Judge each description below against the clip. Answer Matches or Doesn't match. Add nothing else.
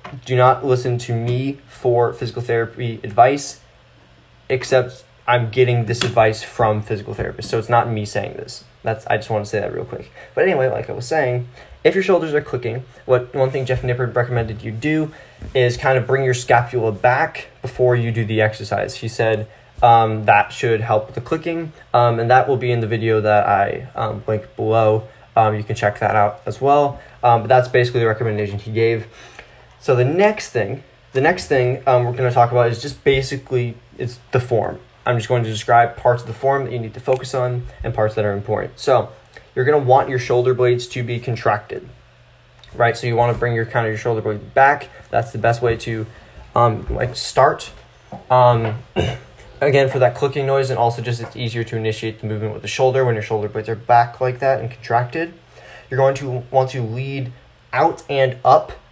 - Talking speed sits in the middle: Doesn't match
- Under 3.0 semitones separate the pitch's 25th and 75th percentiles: Matches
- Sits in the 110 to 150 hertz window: Matches